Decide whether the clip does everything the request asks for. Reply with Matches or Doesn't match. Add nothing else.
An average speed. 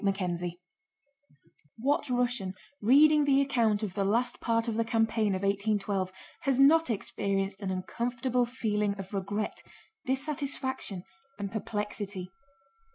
Doesn't match